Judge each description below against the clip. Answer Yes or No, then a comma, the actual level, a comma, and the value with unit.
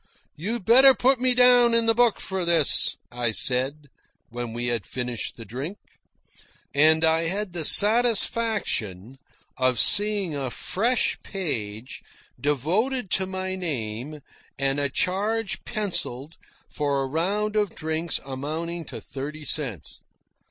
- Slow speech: Yes, slow, 130 wpm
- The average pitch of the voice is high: No, medium, 160 Hz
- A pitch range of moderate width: No, wide, 7.8 semitones